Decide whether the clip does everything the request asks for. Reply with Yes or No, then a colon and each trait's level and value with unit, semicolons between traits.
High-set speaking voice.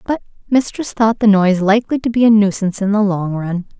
Yes: high, 210 Hz